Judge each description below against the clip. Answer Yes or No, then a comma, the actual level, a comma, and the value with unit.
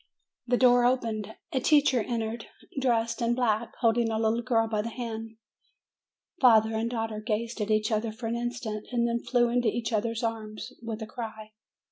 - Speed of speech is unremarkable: Yes, average, 175 wpm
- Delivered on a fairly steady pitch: Yes, narrow, 1.6 semitones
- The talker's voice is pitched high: Yes, high, 230 Hz